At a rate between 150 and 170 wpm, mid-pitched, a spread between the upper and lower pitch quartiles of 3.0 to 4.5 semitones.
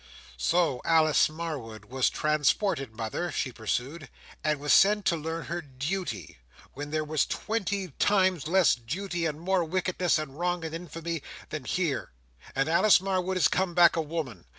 Yes: average, 160 wpm; medium, 160 Hz; average, 4.1 semitones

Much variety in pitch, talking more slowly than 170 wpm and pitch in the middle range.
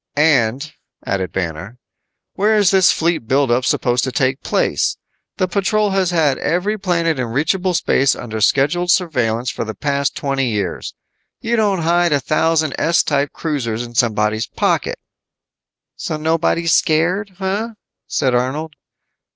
Yes: wide, 6.2 semitones; average, 145 wpm; medium, 150 Hz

